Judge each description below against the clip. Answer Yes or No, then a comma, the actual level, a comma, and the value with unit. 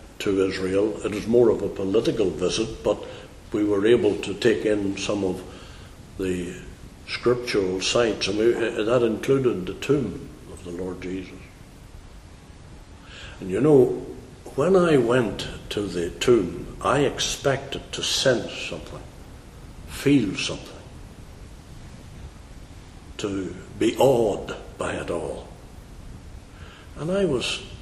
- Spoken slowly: Yes, slow, 120 wpm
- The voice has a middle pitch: No, very low, 95 Hz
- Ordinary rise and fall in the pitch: No, narrow, 2.2 semitones